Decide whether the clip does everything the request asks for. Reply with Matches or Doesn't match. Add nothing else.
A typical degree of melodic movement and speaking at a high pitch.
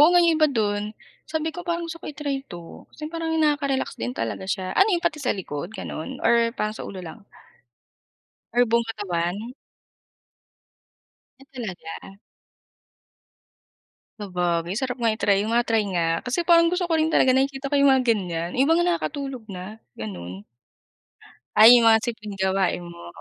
Doesn't match